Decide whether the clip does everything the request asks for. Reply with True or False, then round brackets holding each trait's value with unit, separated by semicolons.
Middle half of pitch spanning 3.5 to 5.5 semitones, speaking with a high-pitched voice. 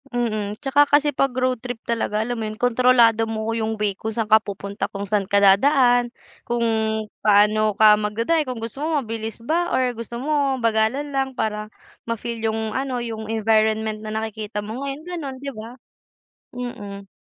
False (2.8 semitones; 225 Hz)